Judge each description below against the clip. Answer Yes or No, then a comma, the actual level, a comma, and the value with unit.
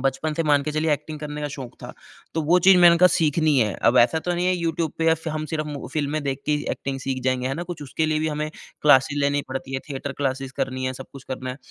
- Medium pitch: Yes, medium, 150 Hz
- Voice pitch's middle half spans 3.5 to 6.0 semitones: No, average, 3.0 semitones